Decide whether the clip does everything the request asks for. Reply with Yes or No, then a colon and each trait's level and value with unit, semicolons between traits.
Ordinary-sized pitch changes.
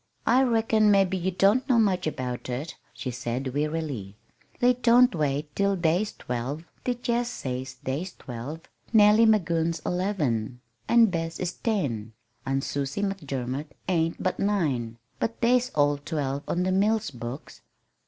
No: wide, 7.5 semitones